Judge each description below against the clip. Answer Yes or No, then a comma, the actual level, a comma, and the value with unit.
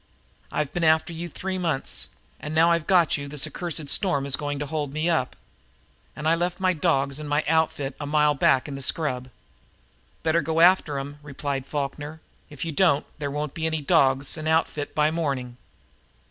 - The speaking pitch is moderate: Yes, medium, 150 Hz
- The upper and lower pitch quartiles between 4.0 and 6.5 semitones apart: No, narrow, 2.5 semitones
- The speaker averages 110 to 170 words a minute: No, average, 190 wpm